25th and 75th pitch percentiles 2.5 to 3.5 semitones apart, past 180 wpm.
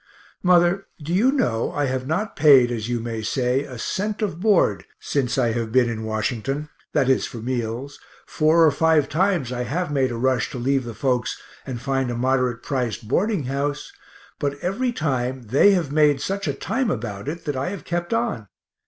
No: wide, 5.4 semitones; average, 195 wpm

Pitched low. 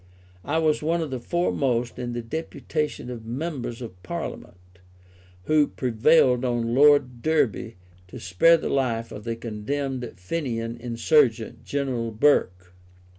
Yes: low, 125 Hz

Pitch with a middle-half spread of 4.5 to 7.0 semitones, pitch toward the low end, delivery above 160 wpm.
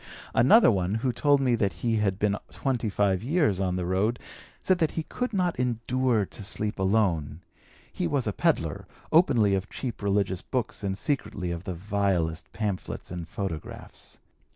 Yes: average, 4.9 semitones; low, 105 Hz; average, 170 wpm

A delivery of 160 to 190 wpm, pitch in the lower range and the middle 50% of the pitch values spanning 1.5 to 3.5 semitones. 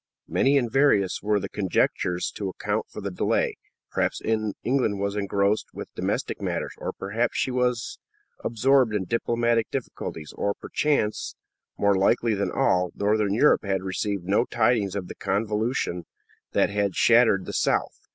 No: average, 150 wpm; low, 105 Hz; average, 2.9 semitones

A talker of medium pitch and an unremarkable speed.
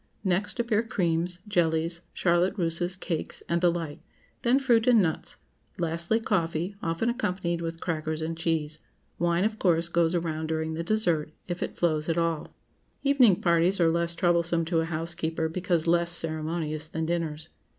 Yes: medium, 170 Hz; average, 160 wpm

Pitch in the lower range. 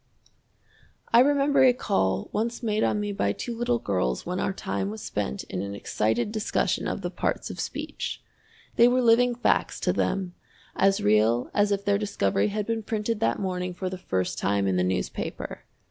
No: high, 195 Hz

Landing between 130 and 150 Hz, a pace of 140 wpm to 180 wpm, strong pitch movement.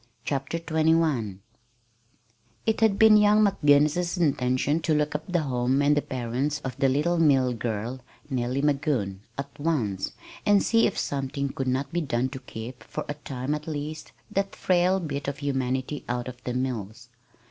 No: medium, 140 Hz; average, 170 wpm; average, 3.9 semitones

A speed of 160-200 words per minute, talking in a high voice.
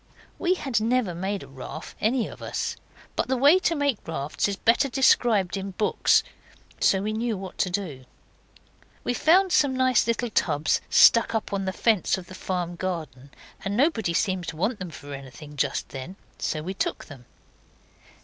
Yes: average, 180 wpm; high, 195 Hz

